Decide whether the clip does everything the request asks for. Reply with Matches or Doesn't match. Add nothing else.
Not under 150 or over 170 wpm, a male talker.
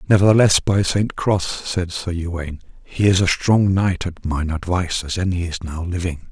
Doesn't match